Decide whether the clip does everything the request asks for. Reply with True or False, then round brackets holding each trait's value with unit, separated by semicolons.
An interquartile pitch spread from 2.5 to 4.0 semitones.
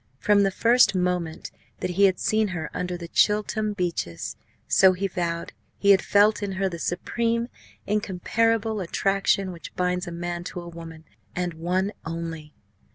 True (3.0 semitones)